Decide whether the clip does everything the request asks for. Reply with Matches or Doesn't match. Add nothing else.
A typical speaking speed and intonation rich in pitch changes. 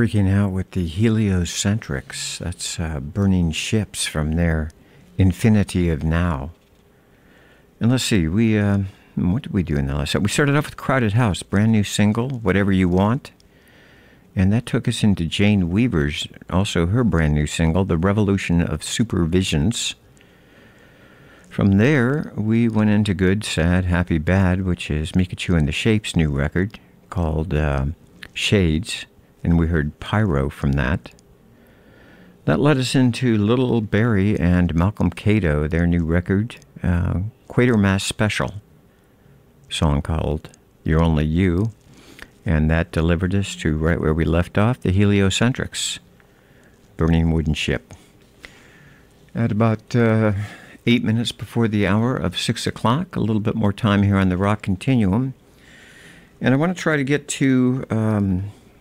Doesn't match